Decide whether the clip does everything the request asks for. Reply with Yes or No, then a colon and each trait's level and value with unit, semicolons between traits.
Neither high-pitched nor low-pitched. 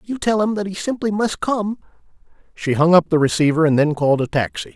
Yes: medium, 175 Hz